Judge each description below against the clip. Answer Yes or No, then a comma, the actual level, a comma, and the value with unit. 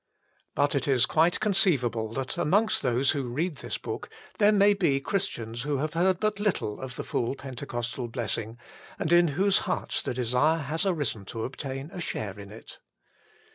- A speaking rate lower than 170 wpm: No, average, 175 wpm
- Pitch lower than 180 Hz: Yes, medium, 140 Hz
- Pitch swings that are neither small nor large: No, wide, 6.5 semitones